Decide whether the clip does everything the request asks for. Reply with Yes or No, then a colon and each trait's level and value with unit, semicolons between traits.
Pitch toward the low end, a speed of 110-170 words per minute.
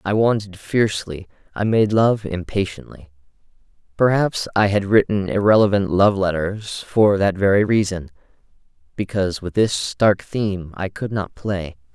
Yes: low, 100 Hz; slow, 135 wpm